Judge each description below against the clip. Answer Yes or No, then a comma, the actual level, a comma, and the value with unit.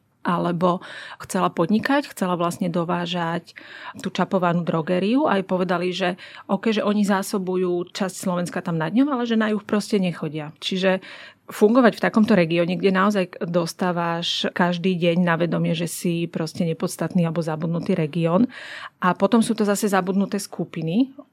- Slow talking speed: No, average, 150 wpm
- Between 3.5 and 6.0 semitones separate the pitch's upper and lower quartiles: No, average, 2.8 semitones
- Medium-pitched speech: Yes, medium, 180 Hz